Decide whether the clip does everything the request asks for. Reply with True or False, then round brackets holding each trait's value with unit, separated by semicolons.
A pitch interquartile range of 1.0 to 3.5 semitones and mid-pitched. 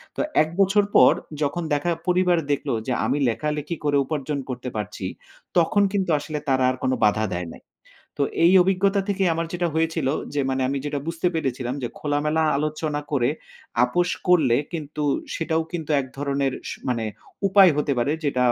False (4.2 semitones; 150 Hz)